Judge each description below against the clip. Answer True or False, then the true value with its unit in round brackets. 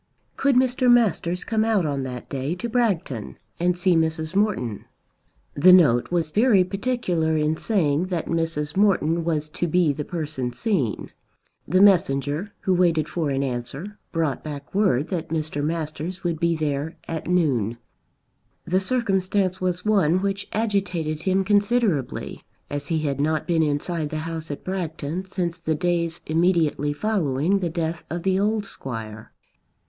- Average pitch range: True (4.1 semitones)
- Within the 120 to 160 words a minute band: True (155 wpm)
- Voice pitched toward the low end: False (170 Hz)